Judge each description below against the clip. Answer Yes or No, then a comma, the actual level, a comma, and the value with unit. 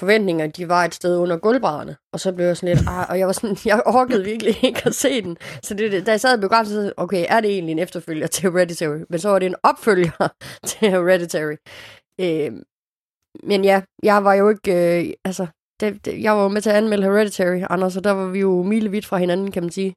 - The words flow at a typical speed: No, fast, 235 wpm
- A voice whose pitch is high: Yes, high, 195 Hz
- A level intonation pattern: No, average, 3.0 semitones